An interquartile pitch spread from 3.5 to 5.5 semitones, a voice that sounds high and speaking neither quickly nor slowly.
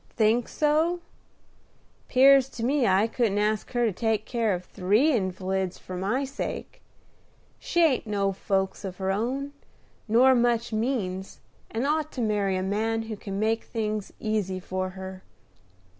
Yes: average, 4.2 semitones; high, 215 Hz; average, 155 wpm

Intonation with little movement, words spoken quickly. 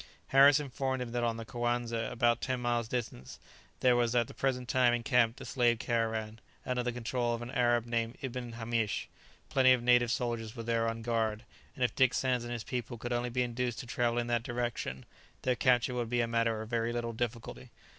Yes: narrow, 1.2 semitones; fast, 215 wpm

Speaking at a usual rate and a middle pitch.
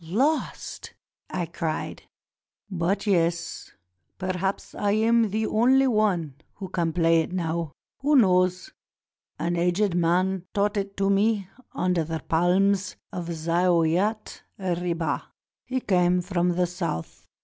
No: slow, 125 wpm; medium, 180 Hz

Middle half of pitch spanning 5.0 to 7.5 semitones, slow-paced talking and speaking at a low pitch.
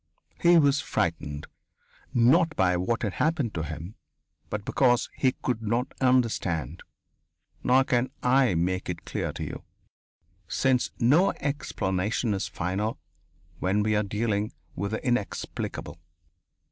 Yes: wide, 5.5 semitones; slow, 130 wpm; low, 110 Hz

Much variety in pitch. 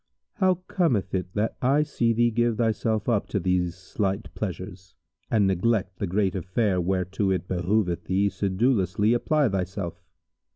No: average, 3.9 semitones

